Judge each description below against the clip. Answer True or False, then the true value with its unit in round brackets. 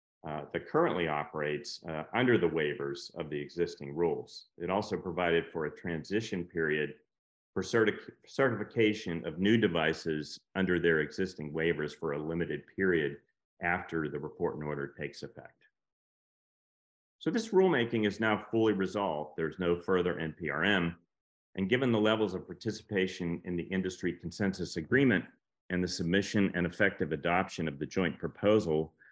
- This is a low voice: True (85 Hz)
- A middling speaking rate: True (150 wpm)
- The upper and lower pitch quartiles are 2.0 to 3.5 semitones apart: False (4.2 semitones)